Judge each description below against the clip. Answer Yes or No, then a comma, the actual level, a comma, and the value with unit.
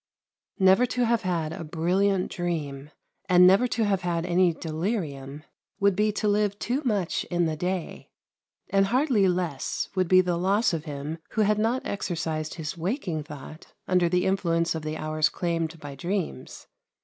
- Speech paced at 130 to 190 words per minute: Yes, average, 170 wpm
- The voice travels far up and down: No, average, 3.8 semitones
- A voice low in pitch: No, medium, 180 Hz